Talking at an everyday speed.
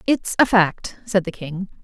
Yes: average, 195 wpm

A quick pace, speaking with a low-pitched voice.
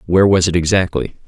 No: average, 190 wpm; very low, 90 Hz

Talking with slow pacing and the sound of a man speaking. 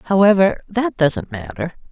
No: slow, 125 wpm; female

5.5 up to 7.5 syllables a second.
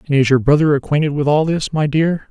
Yes: 6.1 syllables/s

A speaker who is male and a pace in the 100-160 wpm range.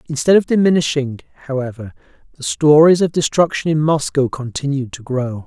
Yes: male; average, 145 wpm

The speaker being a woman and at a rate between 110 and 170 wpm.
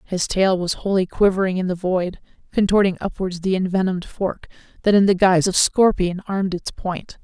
No: female; average, 180 wpm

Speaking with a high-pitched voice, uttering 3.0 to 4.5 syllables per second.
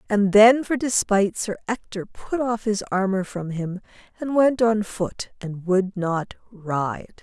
Yes: high, 205 Hz; 4.0 syllables/s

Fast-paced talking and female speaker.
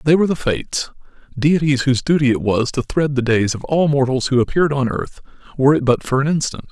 No: fast, 230 wpm; male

